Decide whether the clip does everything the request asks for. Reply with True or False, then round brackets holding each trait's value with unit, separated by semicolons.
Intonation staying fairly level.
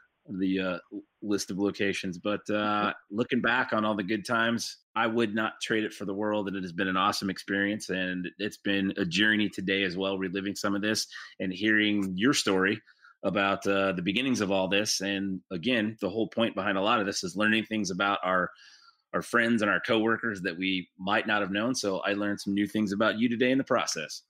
True (2.0 semitones)